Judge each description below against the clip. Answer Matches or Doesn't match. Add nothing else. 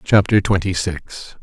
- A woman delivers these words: Doesn't match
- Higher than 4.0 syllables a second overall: Matches